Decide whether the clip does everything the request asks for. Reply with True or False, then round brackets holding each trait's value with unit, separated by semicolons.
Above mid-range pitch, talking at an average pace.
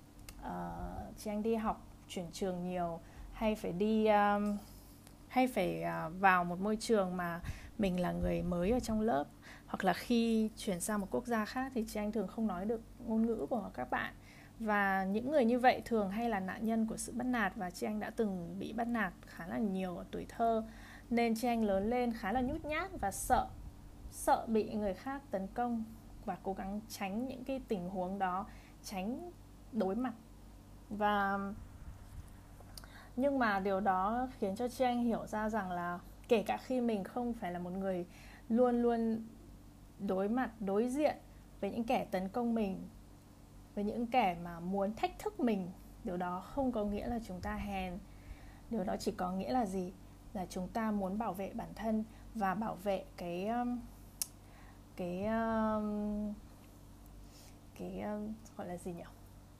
True (205 Hz; 180 wpm)